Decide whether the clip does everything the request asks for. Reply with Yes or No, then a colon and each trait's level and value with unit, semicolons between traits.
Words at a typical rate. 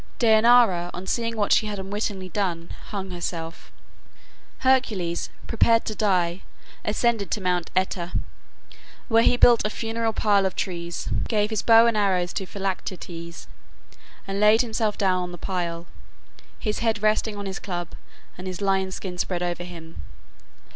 Yes: average, 150 wpm